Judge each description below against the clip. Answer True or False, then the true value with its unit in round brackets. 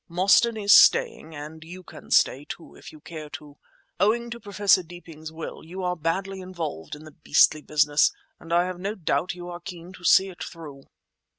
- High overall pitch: False (175 Hz)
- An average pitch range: True (3.3 semitones)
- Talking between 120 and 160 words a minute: False (195 wpm)